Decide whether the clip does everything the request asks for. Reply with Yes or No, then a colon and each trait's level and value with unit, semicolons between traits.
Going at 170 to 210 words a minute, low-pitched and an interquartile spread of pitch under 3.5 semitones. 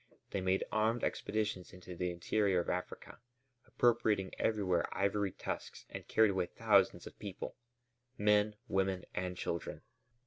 No: slow, 135 wpm; very low, 95 Hz; narrow, 2.6 semitones